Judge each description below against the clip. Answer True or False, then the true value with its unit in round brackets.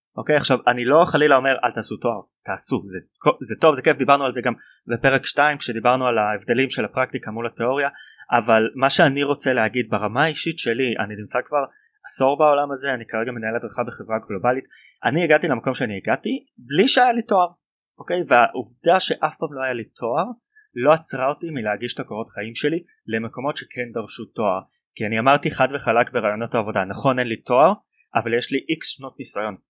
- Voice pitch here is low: True (130 Hz)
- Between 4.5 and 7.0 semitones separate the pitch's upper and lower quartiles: False (3.8 semitones)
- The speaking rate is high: True (195 wpm)